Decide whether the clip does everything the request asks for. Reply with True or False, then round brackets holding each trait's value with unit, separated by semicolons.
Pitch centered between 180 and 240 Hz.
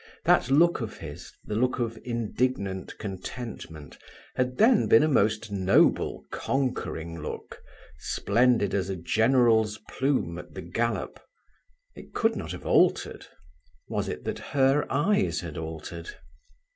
False (110 Hz)